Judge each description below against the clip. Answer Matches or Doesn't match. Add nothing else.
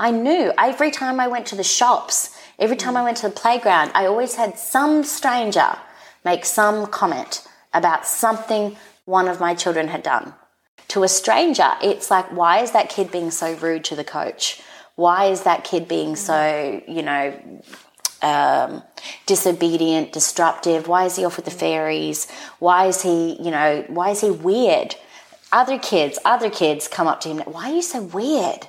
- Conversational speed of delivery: Matches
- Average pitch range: Doesn't match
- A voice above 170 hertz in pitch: Matches